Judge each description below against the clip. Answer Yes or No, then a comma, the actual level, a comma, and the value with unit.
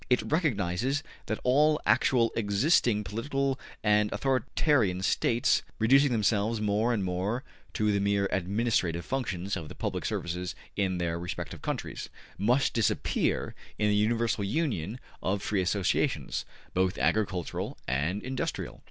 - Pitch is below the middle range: Yes, low, 105 Hz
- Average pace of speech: No, slow, 130 wpm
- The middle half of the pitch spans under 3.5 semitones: No, average, 4.7 semitones